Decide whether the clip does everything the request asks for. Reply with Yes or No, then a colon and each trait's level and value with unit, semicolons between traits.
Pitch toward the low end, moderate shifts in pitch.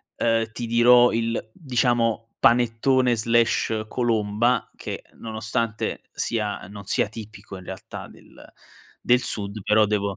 No: low, 115 Hz; narrow, 1.9 semitones